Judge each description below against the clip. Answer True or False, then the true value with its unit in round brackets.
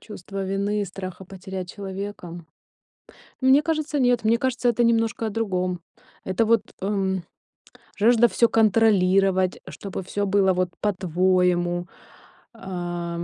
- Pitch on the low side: False (195 Hz)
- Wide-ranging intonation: False (3.6 semitones)